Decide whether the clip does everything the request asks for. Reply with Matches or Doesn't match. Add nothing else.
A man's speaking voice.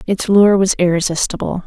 Doesn't match